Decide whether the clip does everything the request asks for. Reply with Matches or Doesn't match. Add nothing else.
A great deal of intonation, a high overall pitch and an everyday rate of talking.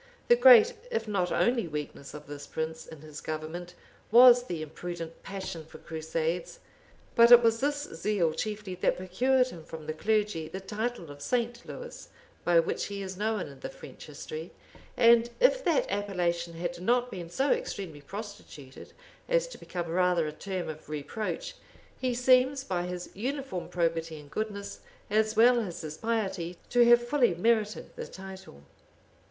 Matches